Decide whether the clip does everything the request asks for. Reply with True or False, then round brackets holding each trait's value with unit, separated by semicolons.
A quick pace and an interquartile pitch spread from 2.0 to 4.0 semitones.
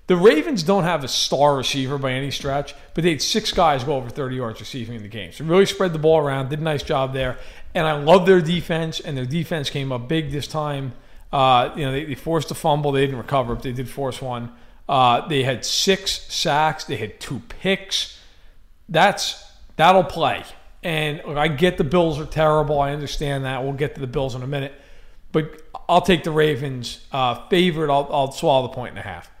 True (220 wpm; 3.5 semitones)